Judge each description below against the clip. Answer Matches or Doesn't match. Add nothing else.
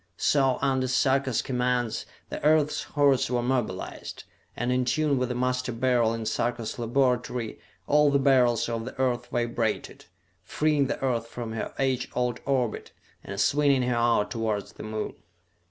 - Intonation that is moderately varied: Doesn't match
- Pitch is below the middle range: Matches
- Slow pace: Doesn't match